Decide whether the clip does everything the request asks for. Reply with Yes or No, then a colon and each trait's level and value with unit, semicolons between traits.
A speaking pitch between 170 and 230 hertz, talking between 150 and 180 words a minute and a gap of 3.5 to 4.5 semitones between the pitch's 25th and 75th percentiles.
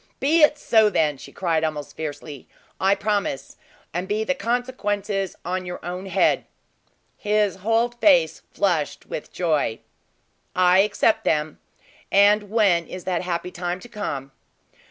No: high, 190 Hz; average, 140 wpm; average, 3.8 semitones